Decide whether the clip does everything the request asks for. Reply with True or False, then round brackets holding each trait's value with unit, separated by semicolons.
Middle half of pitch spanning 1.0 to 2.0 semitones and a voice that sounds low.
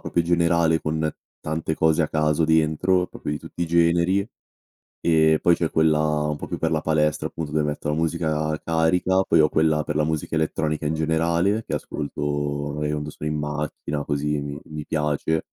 True (1.5 semitones; 80 Hz)